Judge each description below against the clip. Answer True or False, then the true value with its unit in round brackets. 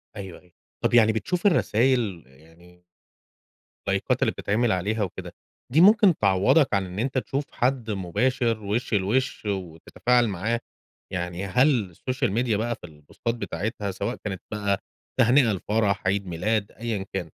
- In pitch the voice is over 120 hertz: False (105 Hz)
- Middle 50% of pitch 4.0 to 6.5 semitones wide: True (4.3 semitones)